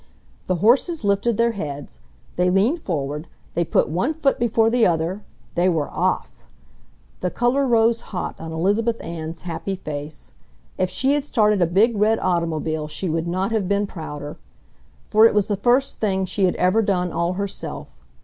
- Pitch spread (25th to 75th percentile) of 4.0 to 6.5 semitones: Yes, average, 5.0 semitones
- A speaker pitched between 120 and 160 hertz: No, high, 190 Hz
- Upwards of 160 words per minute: Yes, average, 175 wpm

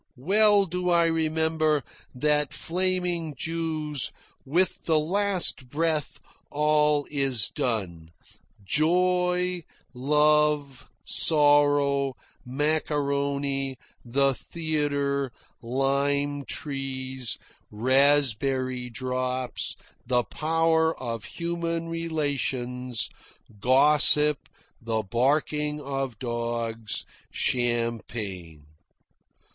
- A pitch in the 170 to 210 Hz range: No, medium, 145 Hz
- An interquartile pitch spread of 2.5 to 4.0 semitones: Yes, average, 3.7 semitones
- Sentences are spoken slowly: Yes, slow, 70 wpm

